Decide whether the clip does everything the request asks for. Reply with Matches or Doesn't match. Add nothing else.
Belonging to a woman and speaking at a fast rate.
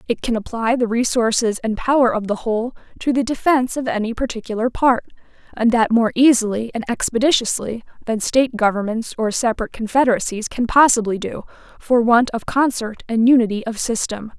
Doesn't match